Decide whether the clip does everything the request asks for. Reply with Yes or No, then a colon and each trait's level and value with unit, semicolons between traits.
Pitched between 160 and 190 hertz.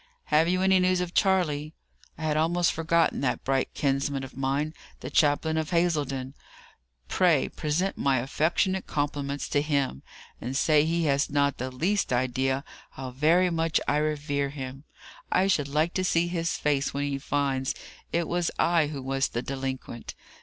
No: medium, 150 Hz